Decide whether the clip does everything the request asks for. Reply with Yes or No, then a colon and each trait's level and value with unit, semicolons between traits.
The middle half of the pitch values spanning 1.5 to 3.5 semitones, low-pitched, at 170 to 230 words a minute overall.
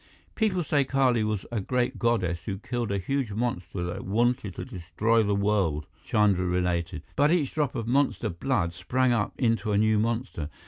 No: average, 5.0 semitones; low, 110 Hz; average, 180 wpm